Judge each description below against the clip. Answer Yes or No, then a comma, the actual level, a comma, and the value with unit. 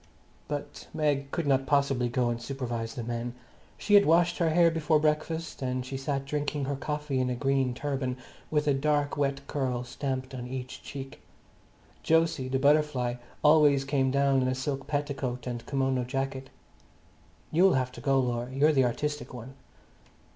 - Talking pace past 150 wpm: Yes, average, 175 wpm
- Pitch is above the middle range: No, low, 135 Hz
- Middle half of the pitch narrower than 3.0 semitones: Yes, narrow, 2.5 semitones